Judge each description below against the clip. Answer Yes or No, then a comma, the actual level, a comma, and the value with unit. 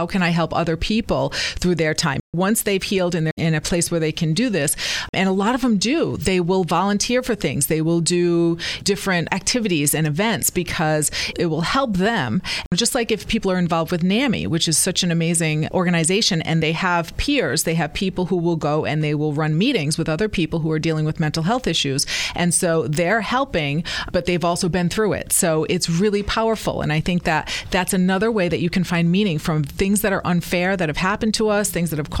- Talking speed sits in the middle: No, fast, 230 wpm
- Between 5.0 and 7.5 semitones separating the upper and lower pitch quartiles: No, average, 3.3 semitones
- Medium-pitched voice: Yes, medium, 175 Hz